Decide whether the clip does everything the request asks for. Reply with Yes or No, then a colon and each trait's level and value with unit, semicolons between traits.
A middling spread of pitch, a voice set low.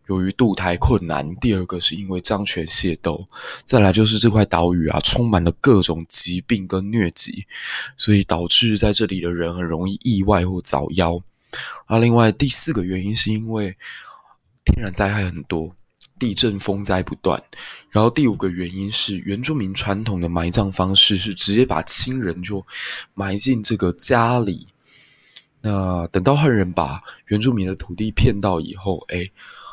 Yes: average, 3.6 semitones; low, 100 Hz